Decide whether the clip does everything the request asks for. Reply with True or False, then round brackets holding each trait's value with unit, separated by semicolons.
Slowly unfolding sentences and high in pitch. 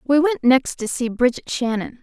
False (210 wpm; 255 Hz)